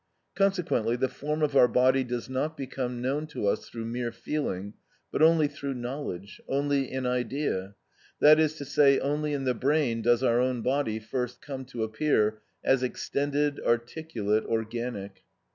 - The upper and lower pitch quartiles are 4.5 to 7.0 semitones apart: No, average, 3.6 semitones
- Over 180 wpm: No, average, 160 wpm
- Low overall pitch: Yes, low, 130 Hz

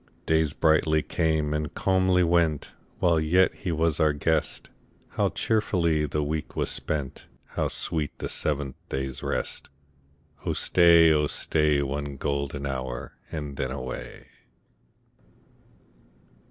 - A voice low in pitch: Yes, very low, 75 Hz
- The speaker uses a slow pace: Yes, slow, 125 wpm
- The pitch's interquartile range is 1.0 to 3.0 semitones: Yes, narrow, 2.5 semitones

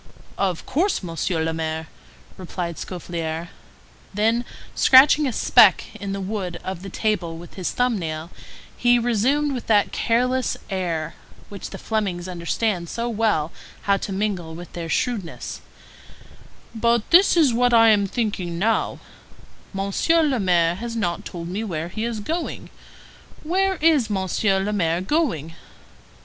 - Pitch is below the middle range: No, high, 200 Hz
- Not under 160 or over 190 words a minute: No, average, 150 wpm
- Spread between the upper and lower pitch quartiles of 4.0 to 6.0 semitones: Yes, wide, 5.4 semitones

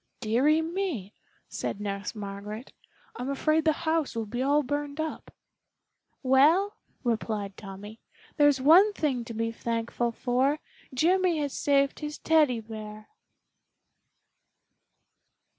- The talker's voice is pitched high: Yes, very high, 265 Hz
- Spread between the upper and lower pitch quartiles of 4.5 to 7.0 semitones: Yes, wide, 5.6 semitones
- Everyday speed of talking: No, slow, 115 wpm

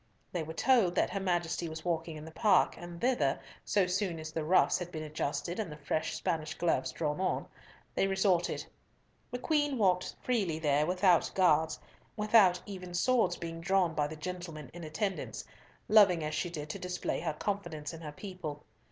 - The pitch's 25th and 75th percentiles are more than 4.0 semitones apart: No, average, 3.5 semitones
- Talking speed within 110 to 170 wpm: No, average, 180 wpm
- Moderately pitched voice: Yes, medium, 175 Hz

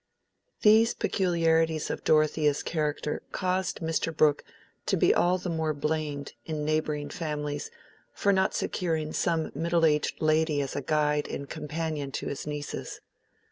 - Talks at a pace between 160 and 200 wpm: No, average, 140 wpm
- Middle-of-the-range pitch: Yes, medium, 155 Hz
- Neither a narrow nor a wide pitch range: No, narrow, 1.8 semitones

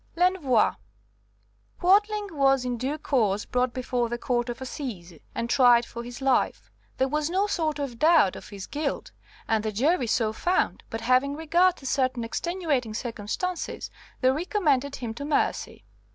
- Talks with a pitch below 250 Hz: No, very high, 265 Hz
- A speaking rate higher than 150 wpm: Yes, average, 160 wpm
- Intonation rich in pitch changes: No, average, 4.8 semitones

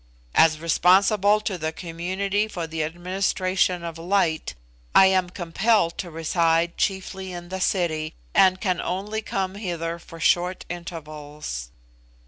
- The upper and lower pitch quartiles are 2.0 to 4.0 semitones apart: Yes, narrow, 2.5 semitones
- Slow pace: Yes, slow, 130 wpm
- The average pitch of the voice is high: No, medium, 175 Hz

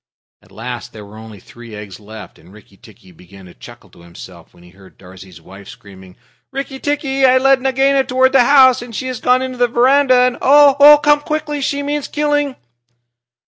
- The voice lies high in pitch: Yes, very high, 250 Hz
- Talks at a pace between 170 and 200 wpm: Yes, average, 195 wpm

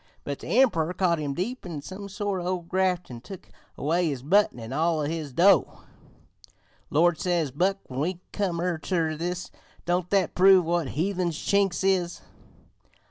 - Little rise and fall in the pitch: No, average, 3.2 semitones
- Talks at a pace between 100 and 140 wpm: No, average, 165 wpm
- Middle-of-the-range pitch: Yes, medium, 175 Hz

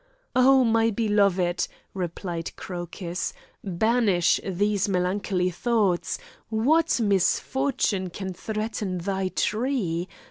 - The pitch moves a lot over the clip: No, average, 3.9 semitones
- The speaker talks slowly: Yes, slow, 85 wpm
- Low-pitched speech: No, high, 200 Hz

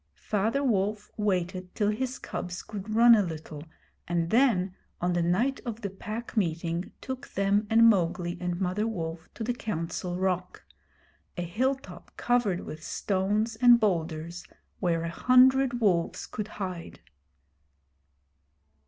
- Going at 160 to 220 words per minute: No, slow, 135 wpm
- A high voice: Yes, high, 195 Hz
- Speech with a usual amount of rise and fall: Yes, average, 4.5 semitones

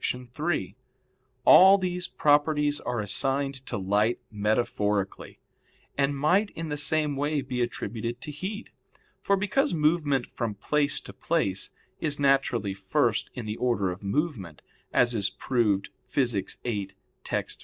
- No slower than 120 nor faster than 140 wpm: Yes, slow, 135 wpm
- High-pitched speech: No, low, 135 Hz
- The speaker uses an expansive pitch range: Yes, wide, 6.2 semitones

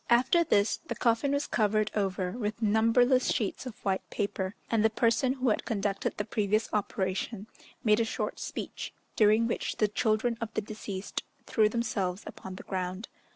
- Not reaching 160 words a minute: No, average, 170 wpm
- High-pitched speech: Yes, high, 215 Hz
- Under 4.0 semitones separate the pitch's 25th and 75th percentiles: Yes, narrow, 2.4 semitones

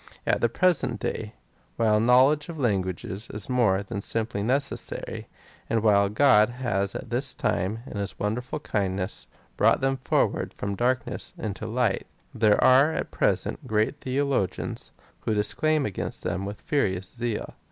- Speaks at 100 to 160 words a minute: Yes, average, 150 wpm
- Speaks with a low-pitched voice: Yes, low, 110 Hz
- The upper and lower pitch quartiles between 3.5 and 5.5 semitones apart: Yes, average, 4.1 semitones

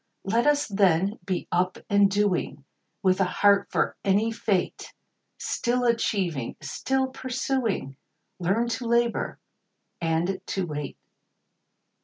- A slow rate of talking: Yes, slow, 115 wpm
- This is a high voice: Yes, high, 200 Hz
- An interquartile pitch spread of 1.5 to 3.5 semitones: No, average, 4.5 semitones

